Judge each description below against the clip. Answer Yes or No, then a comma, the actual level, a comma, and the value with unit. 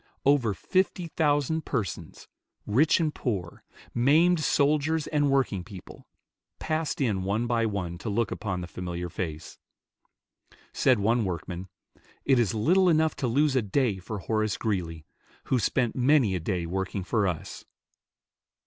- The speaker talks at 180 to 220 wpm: No, average, 145 wpm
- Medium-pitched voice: No, low, 115 Hz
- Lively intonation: Yes, wide, 7.4 semitones